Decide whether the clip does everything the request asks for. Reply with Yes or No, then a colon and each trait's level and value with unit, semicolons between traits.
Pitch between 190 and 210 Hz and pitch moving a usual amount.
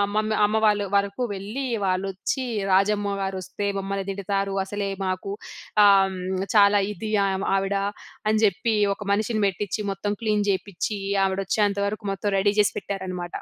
No: high, 200 Hz; narrow, 1.4 semitones